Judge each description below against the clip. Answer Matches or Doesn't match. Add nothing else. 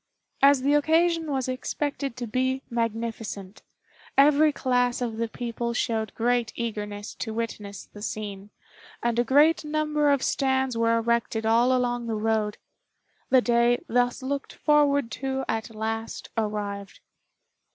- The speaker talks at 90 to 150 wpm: Matches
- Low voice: Doesn't match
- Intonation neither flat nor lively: Matches